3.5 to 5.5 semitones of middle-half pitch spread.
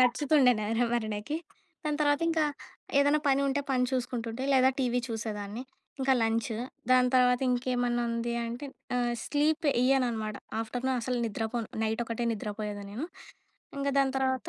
No: average, 2.9 semitones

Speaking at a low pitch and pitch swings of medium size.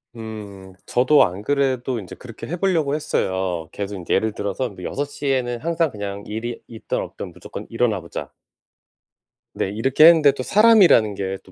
No: low, 115 Hz; wide, 6.1 semitones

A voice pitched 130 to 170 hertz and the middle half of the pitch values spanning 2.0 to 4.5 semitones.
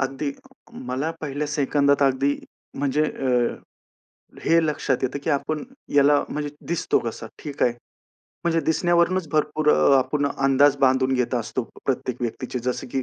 Yes: medium, 140 Hz; narrow, 2.4 semitones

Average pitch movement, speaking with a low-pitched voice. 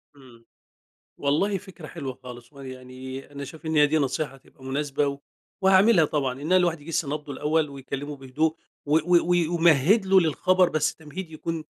No: average, 3.6 semitones; medium, 150 Hz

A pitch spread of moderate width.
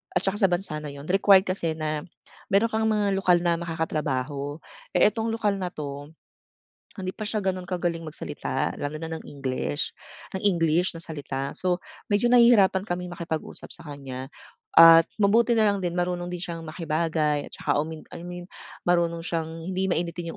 Yes: average, 3.6 semitones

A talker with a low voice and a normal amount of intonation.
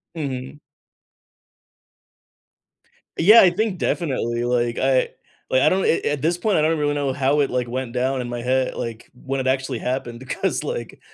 Yes: low, 130 Hz; average, 3.1 semitones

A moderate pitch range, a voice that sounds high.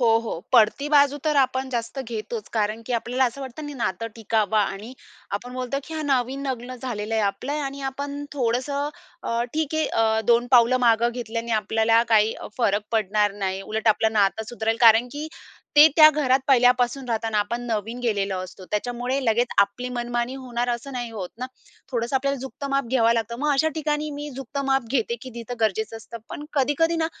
Yes: average, 3.4 semitones; high, 240 Hz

